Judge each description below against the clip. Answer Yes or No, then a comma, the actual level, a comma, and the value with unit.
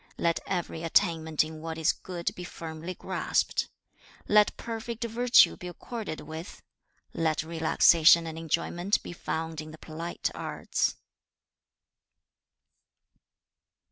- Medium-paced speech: No, slow, 125 wpm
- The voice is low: No, medium, 165 Hz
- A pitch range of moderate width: No, narrow, 2.3 semitones